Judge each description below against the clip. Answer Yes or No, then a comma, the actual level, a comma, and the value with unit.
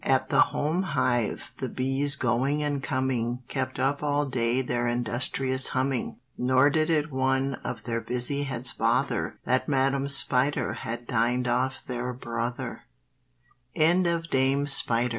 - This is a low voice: Yes, low, 130 Hz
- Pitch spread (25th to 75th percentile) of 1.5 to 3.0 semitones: Yes, narrow, 2.4 semitones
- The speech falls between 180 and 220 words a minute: No, average, 140 wpm